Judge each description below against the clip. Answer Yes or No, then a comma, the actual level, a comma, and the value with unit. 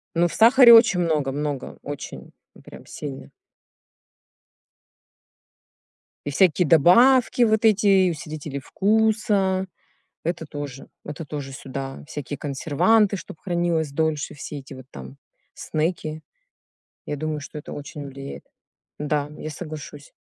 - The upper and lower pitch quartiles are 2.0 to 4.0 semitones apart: No, average, 4.7 semitones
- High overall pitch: No, medium, 155 Hz